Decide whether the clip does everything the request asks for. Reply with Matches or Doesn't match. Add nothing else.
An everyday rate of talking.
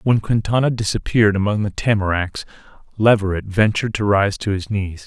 Matches